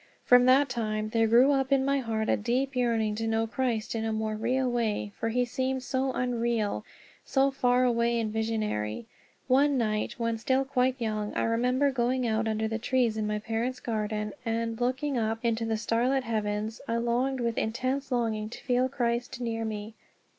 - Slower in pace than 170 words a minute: No, average, 190 wpm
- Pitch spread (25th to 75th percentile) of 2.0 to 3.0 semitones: Yes, narrow, 2.5 semitones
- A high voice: Yes, high, 235 Hz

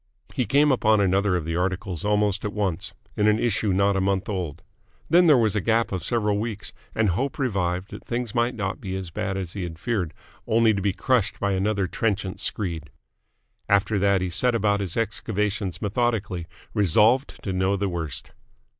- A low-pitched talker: Yes, low, 100 Hz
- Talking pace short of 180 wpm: No, average, 190 wpm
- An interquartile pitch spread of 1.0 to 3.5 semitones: Yes, average, 2.9 semitones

